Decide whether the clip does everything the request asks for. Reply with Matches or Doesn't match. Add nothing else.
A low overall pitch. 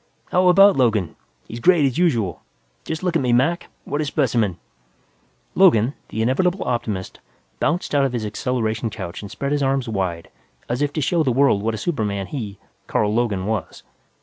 Matches